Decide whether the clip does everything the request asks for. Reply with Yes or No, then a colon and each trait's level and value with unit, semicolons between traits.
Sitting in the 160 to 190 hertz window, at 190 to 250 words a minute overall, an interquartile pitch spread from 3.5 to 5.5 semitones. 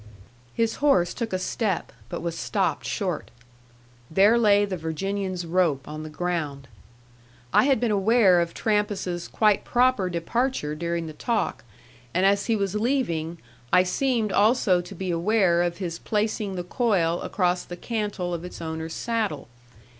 No: medium, 185 Hz; average, 155 wpm; average, 4.1 semitones